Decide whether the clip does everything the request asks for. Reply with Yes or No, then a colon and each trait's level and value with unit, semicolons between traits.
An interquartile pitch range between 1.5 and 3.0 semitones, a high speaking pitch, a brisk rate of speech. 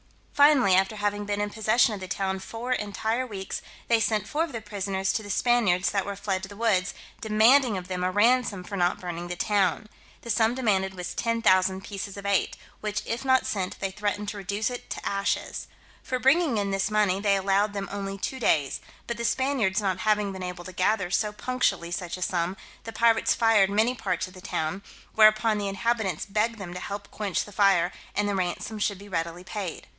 Yes: average, 2.7 semitones; high, 205 Hz; fast, 210 wpm